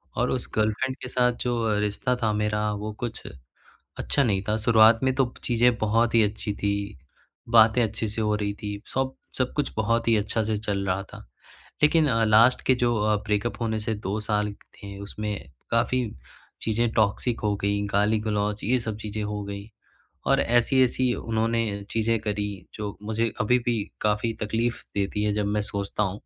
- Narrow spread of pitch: Yes, narrow, 2.2 semitones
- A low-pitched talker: Yes, low, 110 Hz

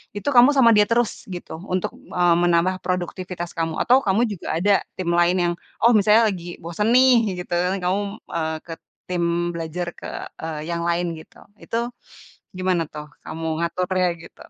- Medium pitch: Yes, medium, 180 Hz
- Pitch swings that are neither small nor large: Yes, average, 3.3 semitones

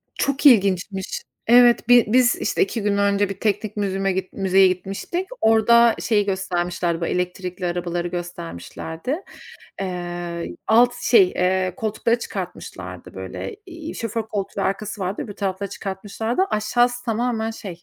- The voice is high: Yes, high, 200 Hz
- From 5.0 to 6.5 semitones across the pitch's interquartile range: No, average, 4.0 semitones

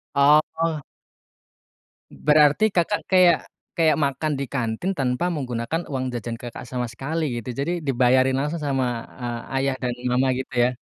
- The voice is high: No, low, 135 Hz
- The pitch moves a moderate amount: Yes, average, 3.7 semitones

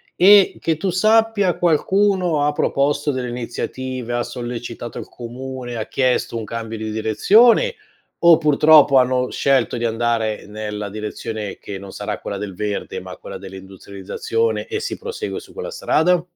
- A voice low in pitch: Yes, low, 125 Hz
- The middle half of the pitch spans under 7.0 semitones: No, wide, 7.7 semitones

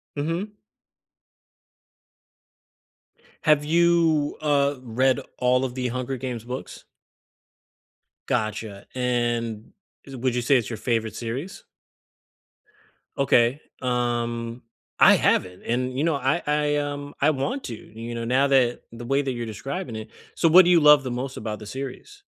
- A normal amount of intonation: Yes, average, 3.5 semitones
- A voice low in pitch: Yes, low, 130 Hz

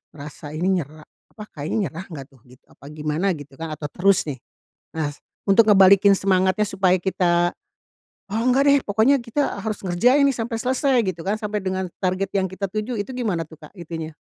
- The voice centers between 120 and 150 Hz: No, high, 190 Hz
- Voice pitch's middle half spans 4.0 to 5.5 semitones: Yes, average, 4.9 semitones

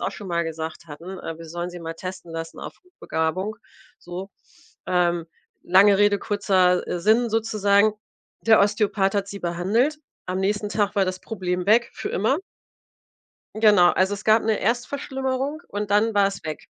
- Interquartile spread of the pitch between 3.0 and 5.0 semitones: Yes, average, 3.4 semitones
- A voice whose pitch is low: No, high, 200 Hz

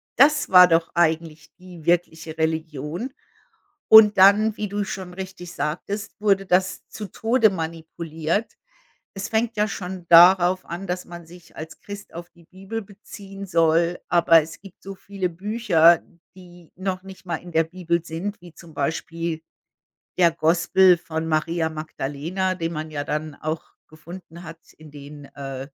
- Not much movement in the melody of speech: No, average, 3.0 semitones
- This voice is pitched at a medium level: Yes, medium, 175 Hz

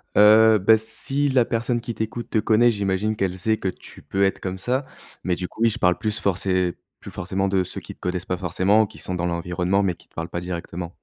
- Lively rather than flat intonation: No, average, 3.5 semitones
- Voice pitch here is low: Yes, very low, 95 Hz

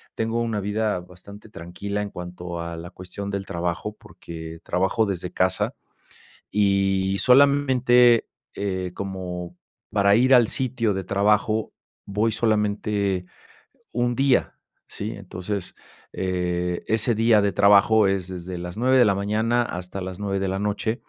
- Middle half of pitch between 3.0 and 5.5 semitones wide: Yes, average, 3.3 semitones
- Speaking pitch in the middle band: No, low, 100 Hz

